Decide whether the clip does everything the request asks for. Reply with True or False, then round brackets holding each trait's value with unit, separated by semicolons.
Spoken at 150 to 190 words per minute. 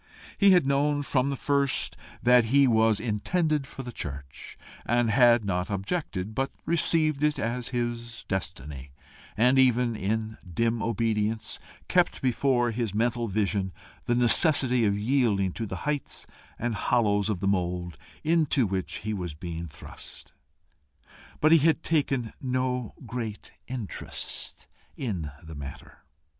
False (140 wpm)